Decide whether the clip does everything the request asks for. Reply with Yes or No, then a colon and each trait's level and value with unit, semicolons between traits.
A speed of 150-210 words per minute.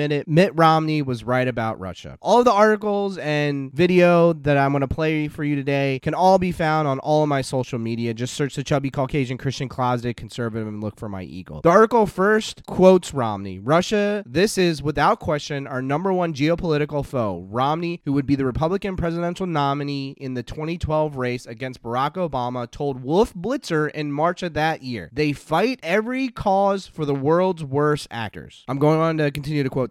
Yes: average, 195 wpm